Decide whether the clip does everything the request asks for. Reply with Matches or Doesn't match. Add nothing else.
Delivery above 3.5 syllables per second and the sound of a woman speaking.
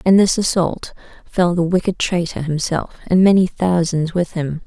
Matches